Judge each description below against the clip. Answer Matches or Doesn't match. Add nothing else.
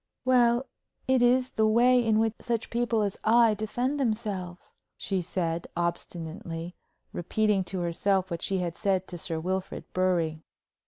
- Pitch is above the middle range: Matches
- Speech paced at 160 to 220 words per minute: Doesn't match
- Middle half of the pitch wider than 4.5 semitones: Matches